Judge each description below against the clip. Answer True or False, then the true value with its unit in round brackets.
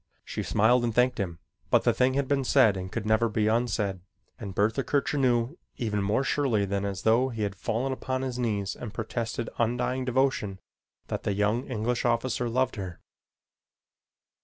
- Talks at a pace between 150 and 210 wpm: True (180 wpm)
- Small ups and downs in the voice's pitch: False (3.6 semitones)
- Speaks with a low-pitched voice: True (115 Hz)